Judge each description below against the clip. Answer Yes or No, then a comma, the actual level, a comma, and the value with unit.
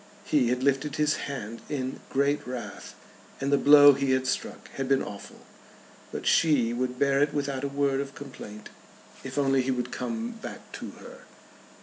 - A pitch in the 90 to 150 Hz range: Yes, low, 135 Hz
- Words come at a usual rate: Yes, average, 180 wpm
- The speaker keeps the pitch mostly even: Yes, narrow, 1.9 semitones